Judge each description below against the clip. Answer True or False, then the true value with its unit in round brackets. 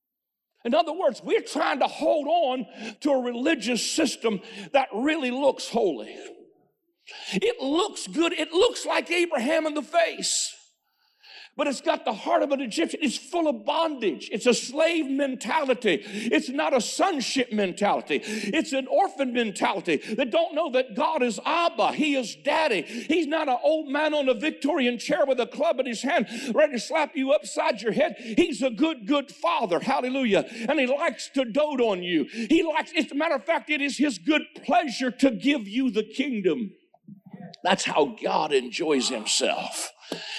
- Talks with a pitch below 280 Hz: False (285 Hz)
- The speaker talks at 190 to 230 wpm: False (175 wpm)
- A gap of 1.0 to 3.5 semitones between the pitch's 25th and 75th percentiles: False (4.5 semitones)